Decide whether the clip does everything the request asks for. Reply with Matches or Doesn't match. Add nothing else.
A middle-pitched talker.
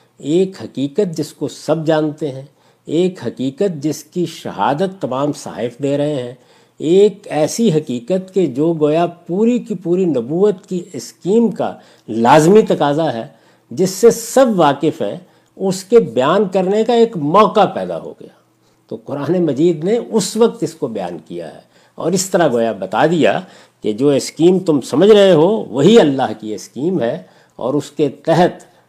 Matches